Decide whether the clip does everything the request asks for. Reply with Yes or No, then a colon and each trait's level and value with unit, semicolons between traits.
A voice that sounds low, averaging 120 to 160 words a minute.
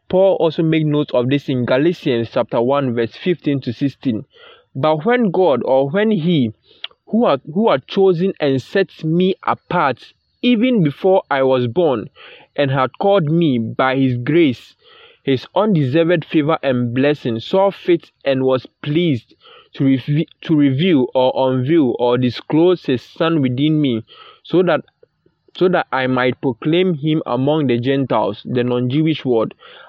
No: medium, 150 Hz; average, 155 wpm